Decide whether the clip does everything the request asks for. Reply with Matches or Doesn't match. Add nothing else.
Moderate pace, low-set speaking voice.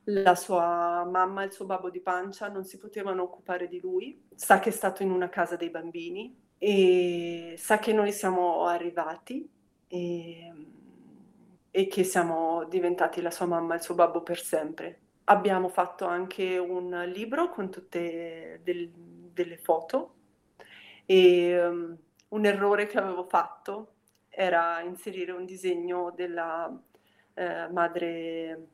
Doesn't match